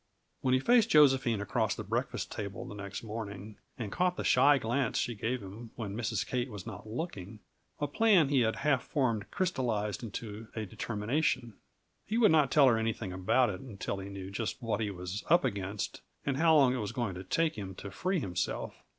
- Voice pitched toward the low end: Yes, low, 115 Hz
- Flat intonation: No, average, 5.1 semitones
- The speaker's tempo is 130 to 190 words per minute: No, average, 200 wpm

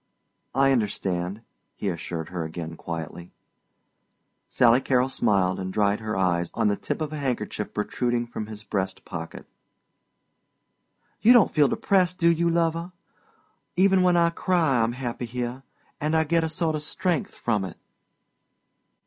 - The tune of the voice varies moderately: No, wide, 8.8 semitones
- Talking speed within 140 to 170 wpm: Yes, average, 150 wpm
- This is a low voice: Yes, low, 120 Hz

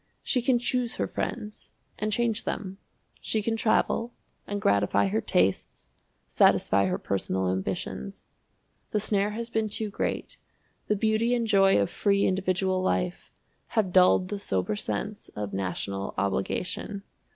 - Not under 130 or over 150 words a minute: Yes, average, 140 wpm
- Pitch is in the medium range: No, high, 195 Hz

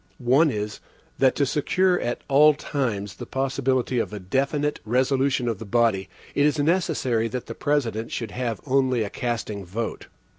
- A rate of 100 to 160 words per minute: No, average, 170 wpm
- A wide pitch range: No, average, 3.9 semitones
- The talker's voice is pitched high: No, low, 125 Hz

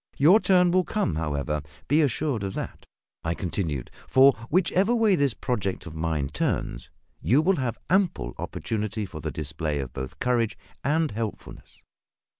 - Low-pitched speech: Yes, low, 115 Hz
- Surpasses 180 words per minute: No, average, 155 wpm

